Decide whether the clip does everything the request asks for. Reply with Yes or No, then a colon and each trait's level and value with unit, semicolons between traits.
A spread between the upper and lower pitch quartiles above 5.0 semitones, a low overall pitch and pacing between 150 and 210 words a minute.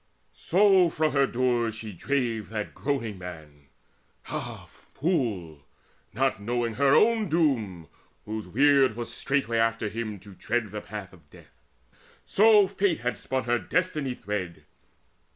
No: wide, 5.4 semitones; low, 115 Hz; slow, 135 wpm